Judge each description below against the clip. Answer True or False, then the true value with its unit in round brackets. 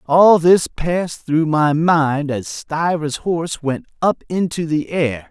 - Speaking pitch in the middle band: True (160 Hz)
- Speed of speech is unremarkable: True (160 wpm)